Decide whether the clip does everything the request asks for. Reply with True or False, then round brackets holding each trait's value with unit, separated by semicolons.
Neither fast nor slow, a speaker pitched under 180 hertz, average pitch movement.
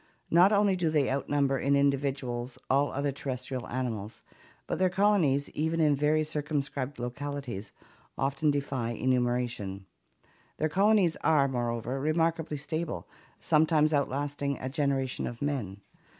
False (125 wpm; 140 Hz; 3.2 semitones)